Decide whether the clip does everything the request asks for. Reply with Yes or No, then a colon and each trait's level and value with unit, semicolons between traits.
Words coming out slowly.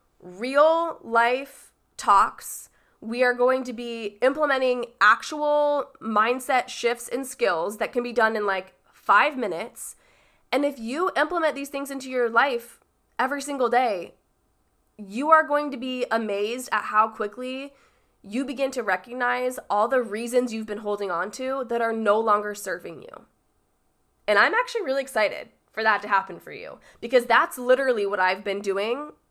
No: average, 160 wpm